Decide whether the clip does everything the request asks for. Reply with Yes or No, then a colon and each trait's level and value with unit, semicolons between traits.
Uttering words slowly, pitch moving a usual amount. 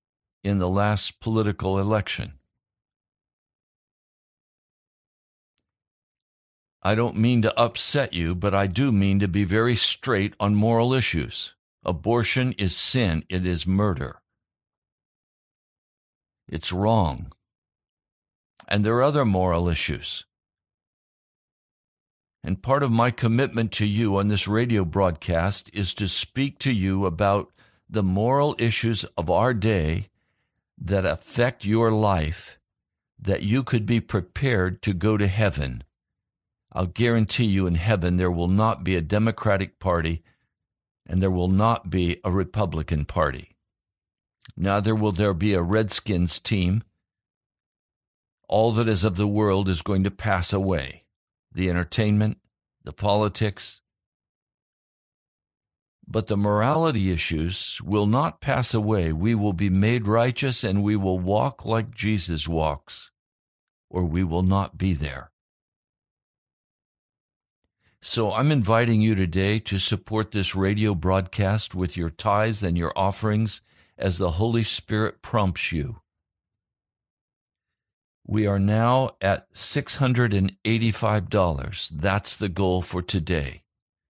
Yes: slow, 125 wpm; average, 3.4 semitones